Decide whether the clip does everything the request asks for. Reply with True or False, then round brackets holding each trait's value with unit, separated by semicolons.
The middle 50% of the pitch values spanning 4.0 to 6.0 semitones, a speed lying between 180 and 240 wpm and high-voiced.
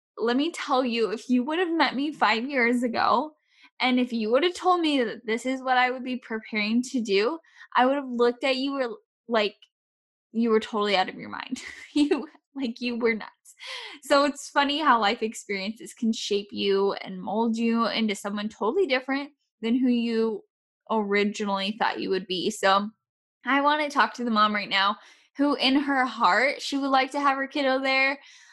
True (4.3 semitones; 200 wpm; 245 Hz)